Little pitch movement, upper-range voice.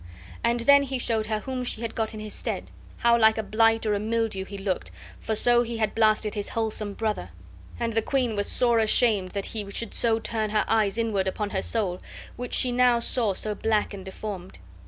Yes: narrow, 2.1 semitones; high, 220 Hz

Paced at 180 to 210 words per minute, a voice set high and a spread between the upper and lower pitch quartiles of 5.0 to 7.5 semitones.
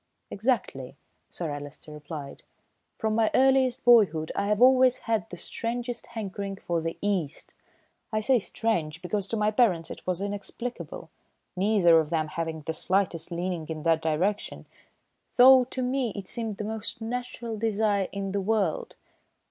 No: average, 155 wpm; high, 200 Hz; wide, 5.6 semitones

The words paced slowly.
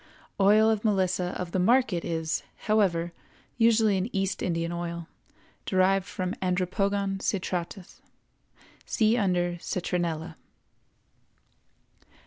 Yes: slow, 100 wpm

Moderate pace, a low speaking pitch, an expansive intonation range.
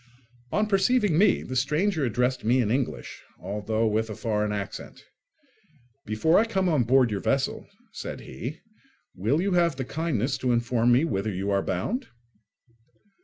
Yes: average, 160 wpm; low, 125 Hz; wide, 7.2 semitones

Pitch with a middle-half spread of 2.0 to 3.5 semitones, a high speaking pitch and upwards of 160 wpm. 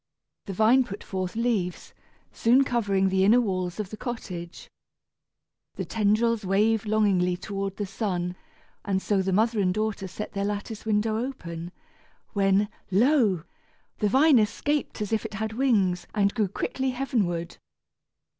No: average, 3.0 semitones; high, 210 Hz; average, 145 wpm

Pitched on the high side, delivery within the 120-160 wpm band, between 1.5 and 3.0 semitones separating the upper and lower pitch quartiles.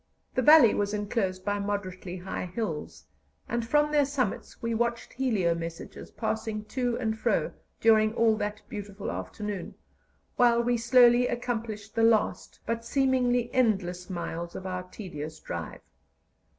No: high, 220 Hz; average, 140 wpm; average, 4.2 semitones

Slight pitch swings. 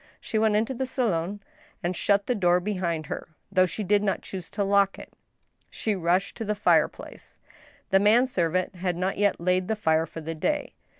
No: average, 3.1 semitones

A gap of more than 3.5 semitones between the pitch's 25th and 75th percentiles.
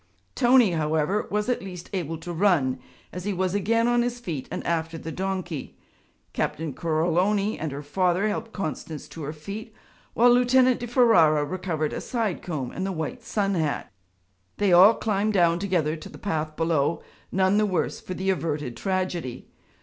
Yes: average, 4.6 semitones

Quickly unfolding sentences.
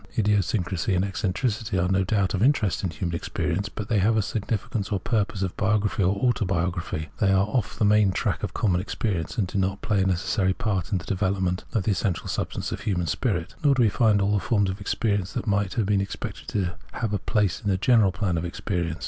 Yes: fast, 235 wpm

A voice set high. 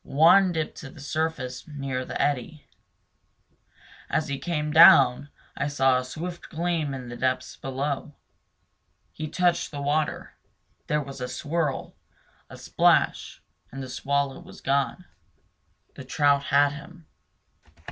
No: medium, 145 Hz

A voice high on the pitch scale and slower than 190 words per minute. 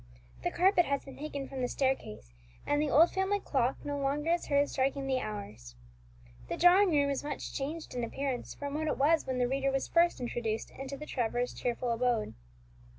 No: very high, 275 Hz; average, 200 wpm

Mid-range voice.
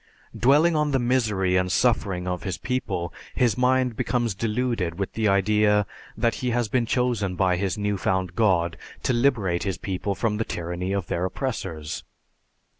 No: low, 105 Hz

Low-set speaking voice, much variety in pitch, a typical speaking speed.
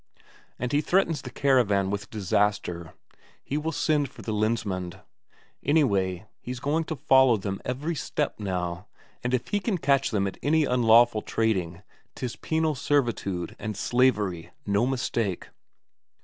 Yes: low, 120 Hz; wide, 6.1 semitones; average, 145 wpm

